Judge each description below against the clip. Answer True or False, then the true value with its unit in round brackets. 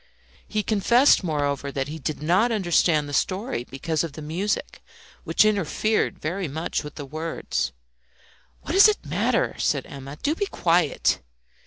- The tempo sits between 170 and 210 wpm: False (155 wpm)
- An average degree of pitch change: False (6.2 semitones)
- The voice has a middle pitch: True (165 Hz)